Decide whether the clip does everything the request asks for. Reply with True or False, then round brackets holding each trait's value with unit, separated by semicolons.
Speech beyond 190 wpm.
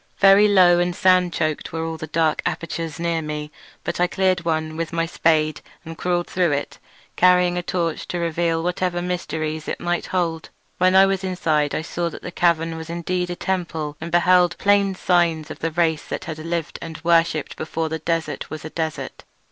True (200 wpm)